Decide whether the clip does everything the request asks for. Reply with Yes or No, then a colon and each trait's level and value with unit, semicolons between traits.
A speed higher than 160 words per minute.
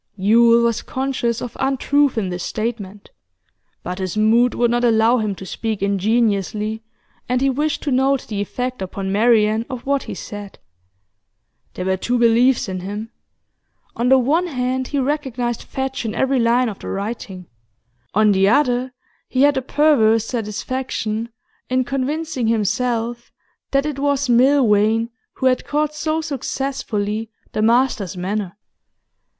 No: average, 150 wpm